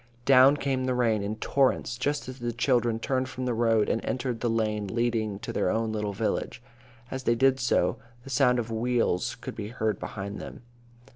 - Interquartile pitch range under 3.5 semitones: Yes, average, 2.7 semitones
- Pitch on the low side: Yes, low, 120 Hz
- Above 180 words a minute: Yes, average, 200 wpm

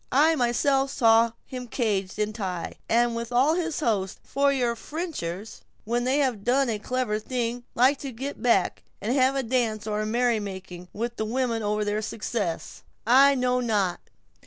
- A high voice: Yes, high, 235 Hz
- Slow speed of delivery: No, average, 175 wpm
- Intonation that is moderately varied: Yes, average, 3.4 semitones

